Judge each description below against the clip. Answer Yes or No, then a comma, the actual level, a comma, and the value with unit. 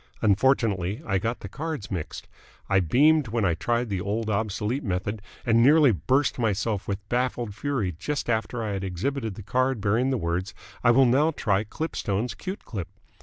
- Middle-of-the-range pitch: No, low, 110 Hz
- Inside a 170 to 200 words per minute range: Yes, average, 175 wpm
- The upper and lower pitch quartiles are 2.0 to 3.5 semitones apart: No, average, 4.5 semitones